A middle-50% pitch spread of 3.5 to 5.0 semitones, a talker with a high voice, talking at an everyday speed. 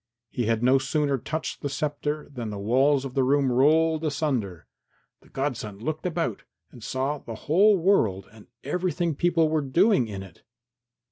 No: average, 4.6 semitones; medium, 140 Hz; average, 165 wpm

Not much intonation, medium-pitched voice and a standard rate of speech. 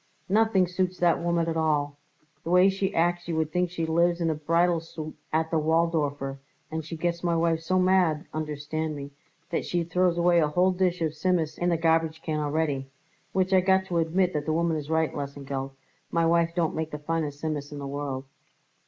No: narrow, 2.3 semitones; medium, 165 Hz; fast, 210 wpm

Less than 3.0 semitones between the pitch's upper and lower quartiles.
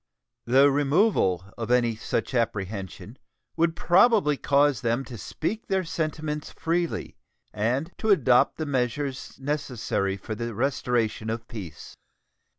No: average, 5.3 semitones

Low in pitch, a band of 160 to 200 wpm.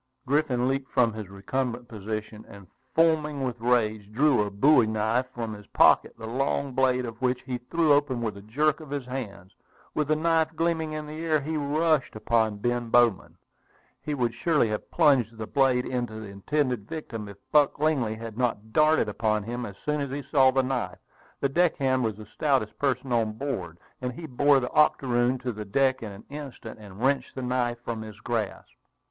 Yes: low, 125 Hz; average, 195 wpm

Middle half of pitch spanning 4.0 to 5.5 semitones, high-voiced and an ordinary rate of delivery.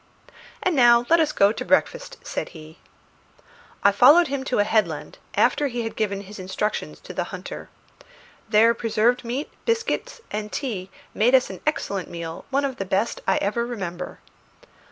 Yes: average, 5.2 semitones; high, 230 Hz; average, 170 wpm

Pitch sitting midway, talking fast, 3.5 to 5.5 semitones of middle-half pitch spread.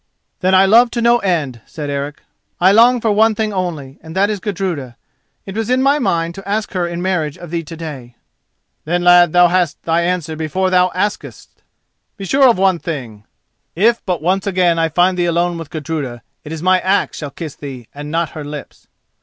Yes: medium, 175 Hz; fast, 210 wpm; average, 3.8 semitones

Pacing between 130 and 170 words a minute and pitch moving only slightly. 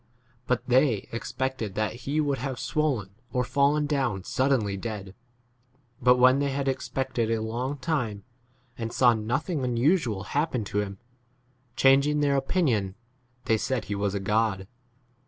No: average, 145 wpm; average, 4.3 semitones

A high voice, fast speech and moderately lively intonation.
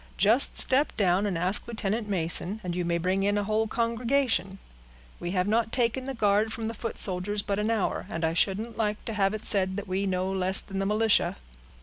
Yes: high, 205 Hz; fast, 220 wpm; average, 3.0 semitones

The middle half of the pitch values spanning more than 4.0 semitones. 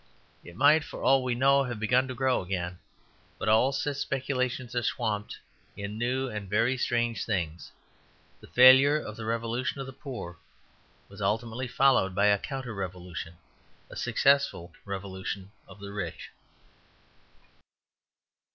Yes: average, 4.8 semitones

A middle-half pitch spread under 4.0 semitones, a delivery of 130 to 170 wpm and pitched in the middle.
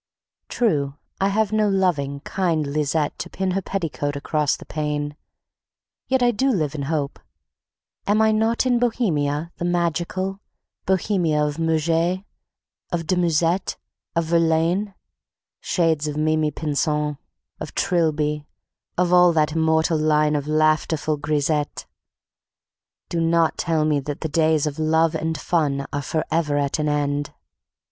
Yes: average, 2.9 semitones; average, 140 wpm; medium, 160 Hz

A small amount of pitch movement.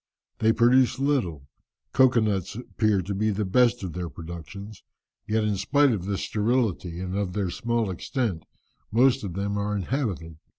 No: average, 4.2 semitones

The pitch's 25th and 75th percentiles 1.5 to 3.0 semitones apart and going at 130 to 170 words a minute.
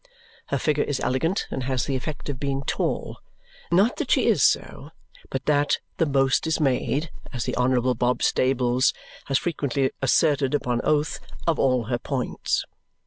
Yes: narrow, 2.6 semitones; average, 165 wpm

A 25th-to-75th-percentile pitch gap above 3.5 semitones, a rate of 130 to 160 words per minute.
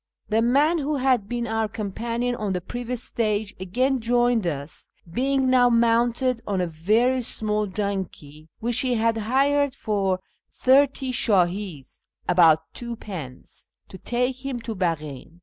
Yes: average, 4.7 semitones; average, 140 wpm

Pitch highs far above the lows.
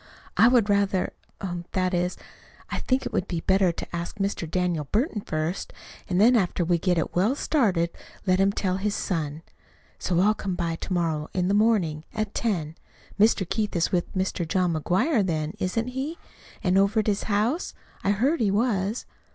No: average, 3.7 semitones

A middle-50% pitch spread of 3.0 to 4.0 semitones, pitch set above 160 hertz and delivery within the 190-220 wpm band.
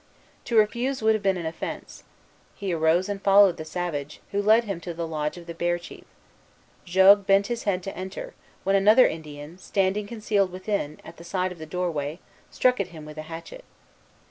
Yes: average, 3.6 semitones; medium, 185 Hz; average, 195 wpm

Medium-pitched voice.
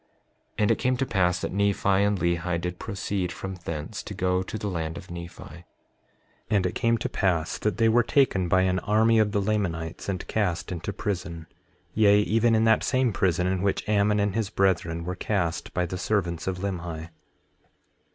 No: very low, 95 Hz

